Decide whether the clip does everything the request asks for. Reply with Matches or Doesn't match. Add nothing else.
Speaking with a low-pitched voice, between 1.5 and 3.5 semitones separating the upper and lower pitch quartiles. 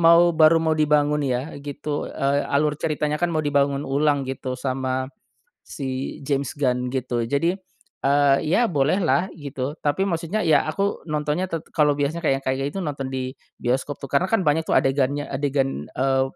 Doesn't match